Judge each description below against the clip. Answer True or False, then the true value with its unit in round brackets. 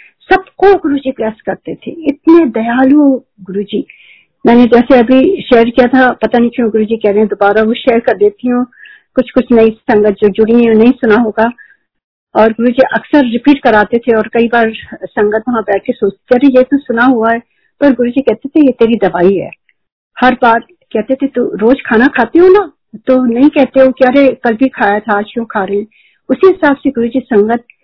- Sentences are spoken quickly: True (215 wpm)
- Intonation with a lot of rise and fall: False (3.2 semitones)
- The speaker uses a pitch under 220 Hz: False (240 Hz)